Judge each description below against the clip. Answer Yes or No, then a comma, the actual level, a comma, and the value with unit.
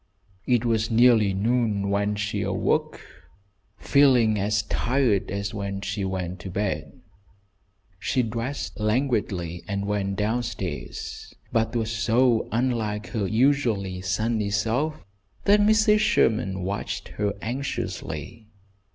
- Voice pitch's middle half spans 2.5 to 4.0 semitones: Yes, average, 3.4 semitones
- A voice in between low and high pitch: No, low, 110 Hz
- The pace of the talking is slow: Yes, slow, 115 wpm